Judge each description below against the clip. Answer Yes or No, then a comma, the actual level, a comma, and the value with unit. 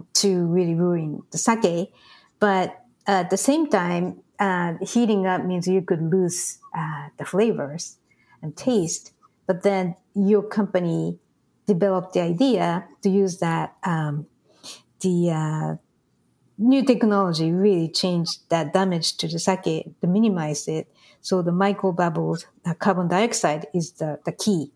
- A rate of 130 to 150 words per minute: Yes, average, 145 wpm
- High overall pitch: No, medium, 180 Hz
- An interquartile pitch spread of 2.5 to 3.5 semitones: Yes, average, 3.1 semitones